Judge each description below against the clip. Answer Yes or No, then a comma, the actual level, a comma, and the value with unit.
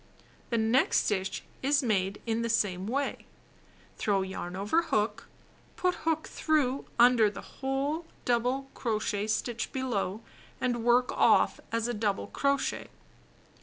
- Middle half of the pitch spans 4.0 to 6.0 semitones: Yes, average, 4.3 semitones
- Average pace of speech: No, slow, 130 wpm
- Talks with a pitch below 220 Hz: No, high, 235 Hz